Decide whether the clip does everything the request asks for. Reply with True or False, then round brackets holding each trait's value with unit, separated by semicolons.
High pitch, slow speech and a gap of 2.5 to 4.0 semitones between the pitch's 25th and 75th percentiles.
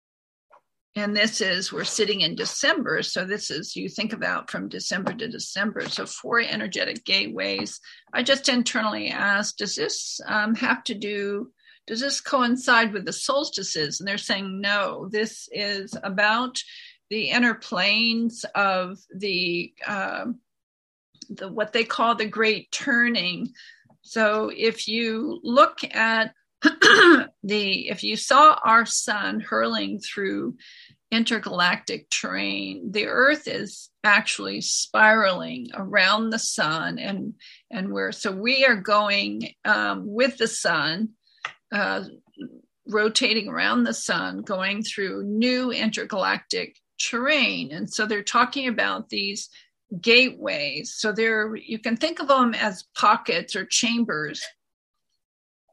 True (225 Hz; 130 wpm; 3.3 semitones)